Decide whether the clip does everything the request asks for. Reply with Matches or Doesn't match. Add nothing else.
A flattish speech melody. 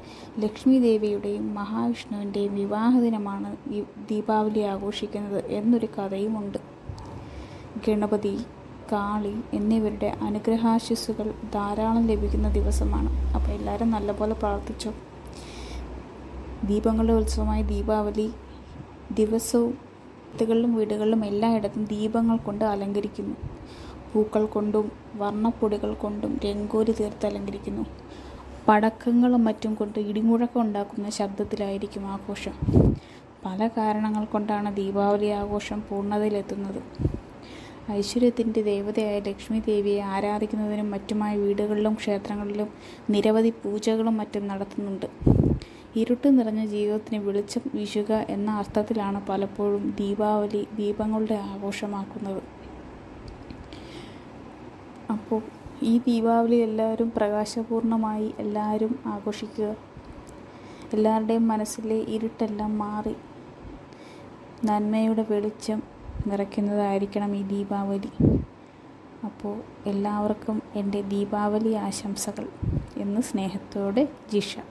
Matches